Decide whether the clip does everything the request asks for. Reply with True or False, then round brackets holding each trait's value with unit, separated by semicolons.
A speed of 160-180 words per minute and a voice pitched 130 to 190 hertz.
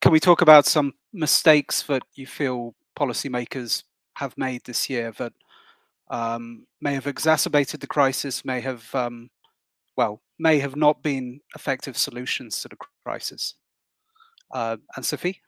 False (145 wpm; 140 Hz)